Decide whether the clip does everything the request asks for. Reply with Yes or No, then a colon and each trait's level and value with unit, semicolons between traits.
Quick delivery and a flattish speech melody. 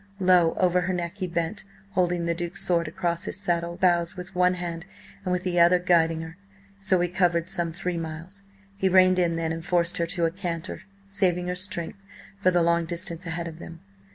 Yes: fast, 210 wpm; narrow, 1.5 semitones